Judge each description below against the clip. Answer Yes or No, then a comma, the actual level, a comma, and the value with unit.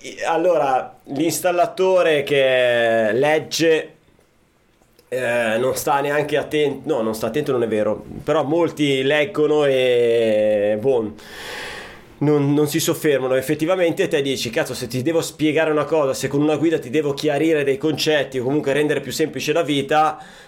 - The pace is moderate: Yes, average, 150 wpm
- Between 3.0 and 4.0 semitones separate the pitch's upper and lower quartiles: Yes, average, 3.4 semitones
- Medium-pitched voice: Yes, medium, 150 Hz